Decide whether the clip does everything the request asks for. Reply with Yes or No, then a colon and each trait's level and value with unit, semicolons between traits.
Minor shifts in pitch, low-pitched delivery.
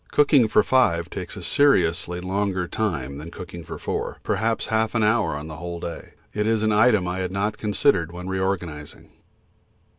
No: average, 4.1 semitones; very low, 95 Hz